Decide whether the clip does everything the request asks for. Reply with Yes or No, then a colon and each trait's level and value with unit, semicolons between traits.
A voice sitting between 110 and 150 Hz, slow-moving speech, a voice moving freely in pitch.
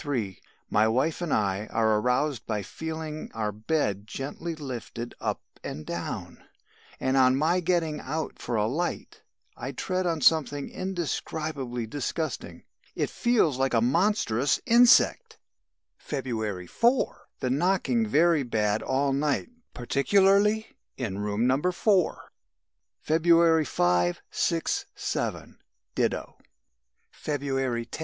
Yes: medium, 140 Hz; slow, 120 wpm; wide, 6.4 semitones